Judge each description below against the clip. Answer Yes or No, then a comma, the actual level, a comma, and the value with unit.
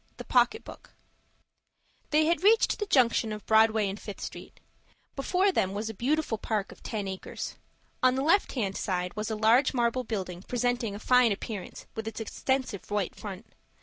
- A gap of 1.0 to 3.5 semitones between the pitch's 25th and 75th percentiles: No, average, 4.1 semitones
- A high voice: Yes, high, 225 Hz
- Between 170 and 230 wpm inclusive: Yes, average, 180 wpm